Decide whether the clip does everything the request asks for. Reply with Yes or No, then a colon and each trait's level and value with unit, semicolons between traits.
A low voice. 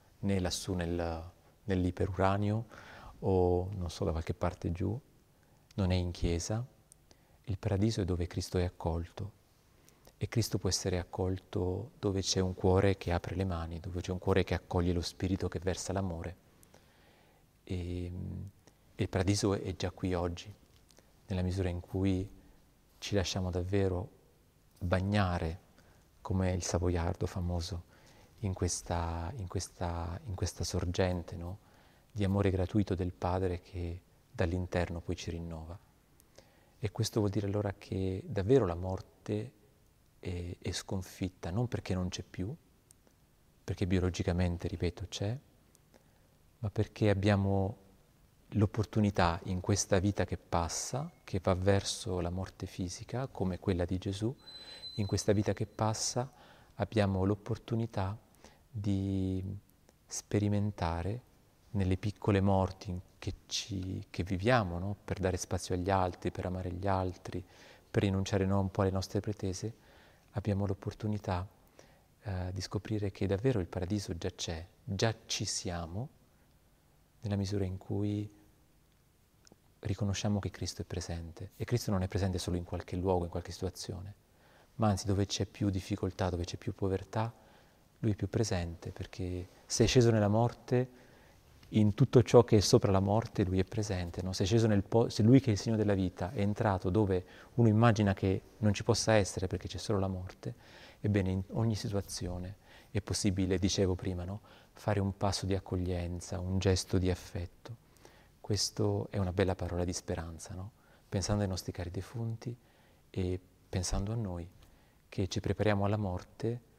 Yes: very low, 95 Hz